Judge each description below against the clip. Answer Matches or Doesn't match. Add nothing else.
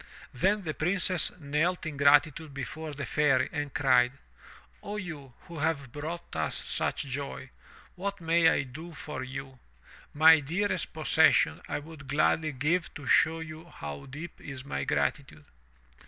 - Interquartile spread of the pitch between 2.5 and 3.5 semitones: Matches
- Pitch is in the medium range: Matches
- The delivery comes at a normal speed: Matches